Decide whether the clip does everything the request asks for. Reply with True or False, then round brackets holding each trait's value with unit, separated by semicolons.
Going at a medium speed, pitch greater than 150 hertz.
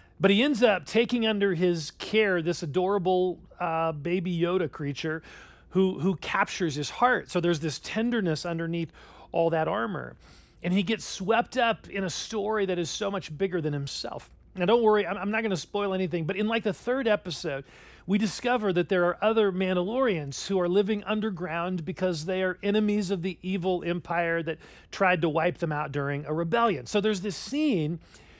True (190 wpm; 185 Hz)